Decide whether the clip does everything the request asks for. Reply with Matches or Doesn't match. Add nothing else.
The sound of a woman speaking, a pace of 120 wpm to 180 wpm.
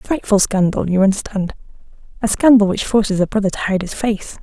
Doesn't match